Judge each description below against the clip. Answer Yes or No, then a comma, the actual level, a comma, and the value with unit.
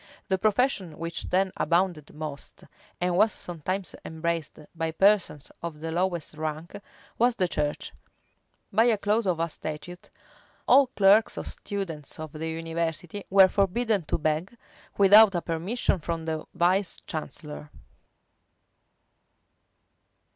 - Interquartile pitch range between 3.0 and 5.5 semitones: Yes, average, 3.7 semitones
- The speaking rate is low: Yes, slow, 125 wpm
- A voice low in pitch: No, medium, 175 Hz